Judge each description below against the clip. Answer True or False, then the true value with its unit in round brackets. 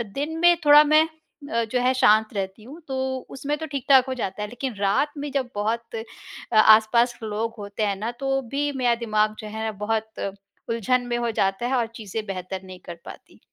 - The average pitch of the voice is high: True (235 Hz)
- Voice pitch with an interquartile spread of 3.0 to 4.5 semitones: True (4.0 semitones)